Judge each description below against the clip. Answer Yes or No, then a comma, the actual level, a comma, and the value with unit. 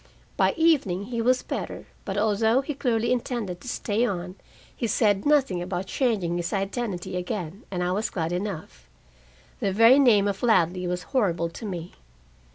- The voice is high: Yes, high, 200 Hz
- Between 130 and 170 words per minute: Yes, average, 165 wpm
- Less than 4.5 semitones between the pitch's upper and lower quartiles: No, average, 4.8 semitones